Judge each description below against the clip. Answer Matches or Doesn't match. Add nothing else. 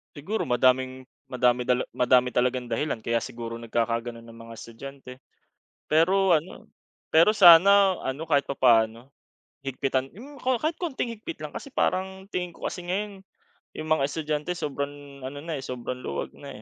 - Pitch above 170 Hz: Doesn't match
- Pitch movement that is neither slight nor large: Doesn't match